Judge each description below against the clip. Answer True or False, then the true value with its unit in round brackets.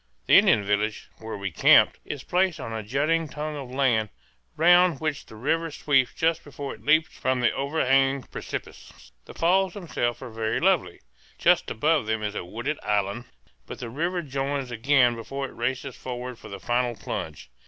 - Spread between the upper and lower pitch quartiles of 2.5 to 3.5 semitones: False (5.1 semitones)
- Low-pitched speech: True (130 Hz)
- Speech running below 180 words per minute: False (185 wpm)